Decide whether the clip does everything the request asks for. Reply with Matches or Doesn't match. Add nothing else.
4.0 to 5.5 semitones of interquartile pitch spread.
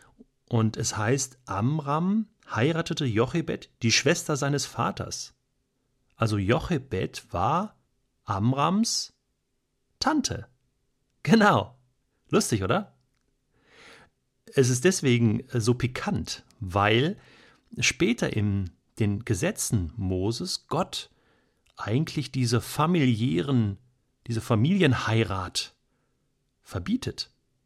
Matches